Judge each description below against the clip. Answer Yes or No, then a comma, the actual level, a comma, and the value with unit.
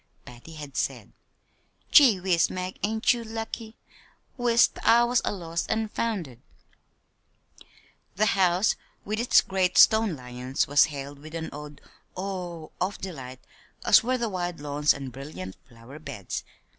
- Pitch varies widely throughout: Yes, wide, 7.3 semitones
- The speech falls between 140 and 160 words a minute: Yes, average, 145 wpm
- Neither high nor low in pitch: Yes, medium, 175 Hz